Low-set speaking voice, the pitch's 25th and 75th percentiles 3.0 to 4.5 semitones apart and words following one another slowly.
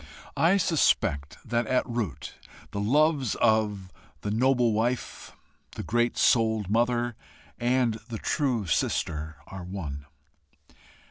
Yes: low, 115 Hz; average, 3.8 semitones; slow, 115 wpm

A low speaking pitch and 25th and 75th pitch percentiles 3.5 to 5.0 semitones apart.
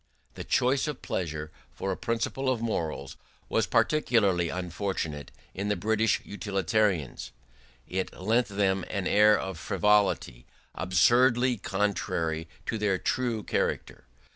Yes: low, 100 Hz; average, 4.0 semitones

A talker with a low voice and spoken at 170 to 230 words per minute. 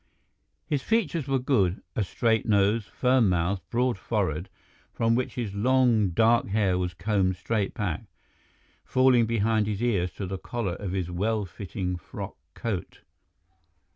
No: low, 105 Hz; average, 140 wpm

